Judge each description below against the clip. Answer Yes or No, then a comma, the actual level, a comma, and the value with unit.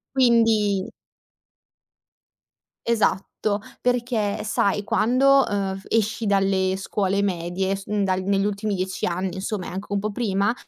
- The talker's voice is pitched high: Yes, high, 200 Hz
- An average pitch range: No, narrow, 2.2 semitones